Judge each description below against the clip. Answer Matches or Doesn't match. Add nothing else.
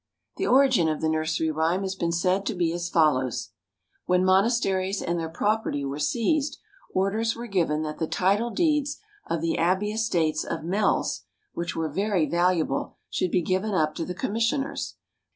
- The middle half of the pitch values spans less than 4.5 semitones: Doesn't match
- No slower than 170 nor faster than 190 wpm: Matches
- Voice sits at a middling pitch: Matches